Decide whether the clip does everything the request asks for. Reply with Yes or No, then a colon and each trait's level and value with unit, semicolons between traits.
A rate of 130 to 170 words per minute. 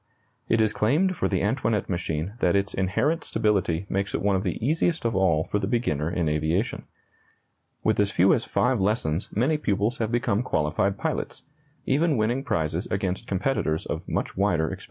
No: average, 180 wpm